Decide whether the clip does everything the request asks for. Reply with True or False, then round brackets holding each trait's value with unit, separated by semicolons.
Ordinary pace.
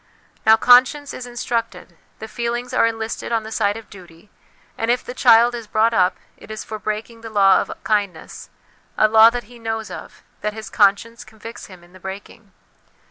True (190 wpm)